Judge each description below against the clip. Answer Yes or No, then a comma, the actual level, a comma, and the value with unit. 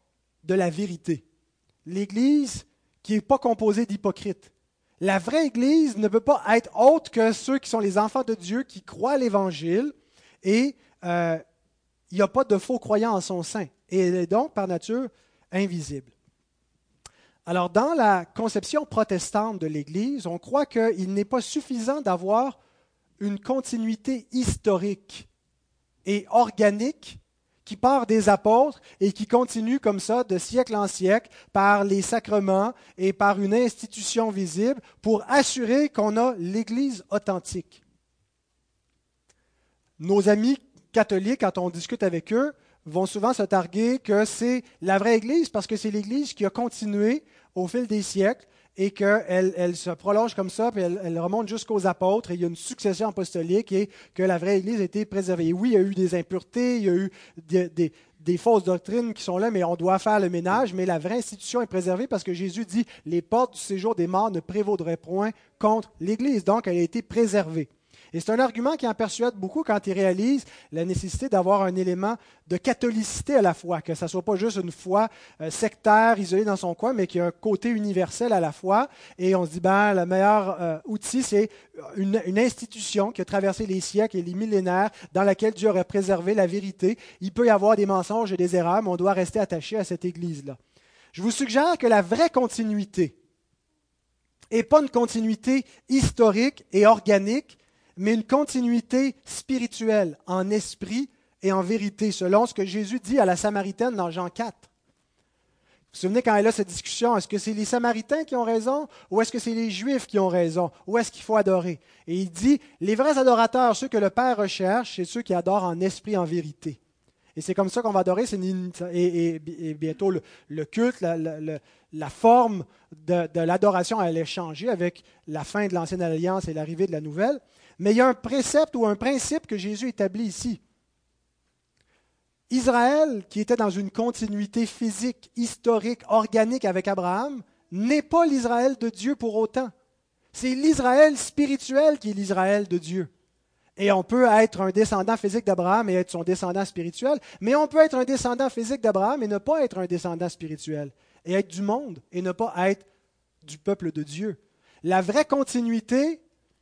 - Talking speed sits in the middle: Yes, average, 190 wpm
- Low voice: No, high, 205 Hz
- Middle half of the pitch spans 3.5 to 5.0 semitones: Yes, average, 4.4 semitones